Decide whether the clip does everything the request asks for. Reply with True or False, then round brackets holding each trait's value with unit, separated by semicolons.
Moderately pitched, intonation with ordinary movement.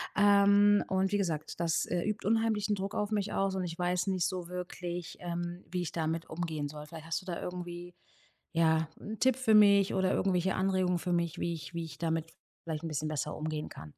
True (175 Hz; 3.0 semitones)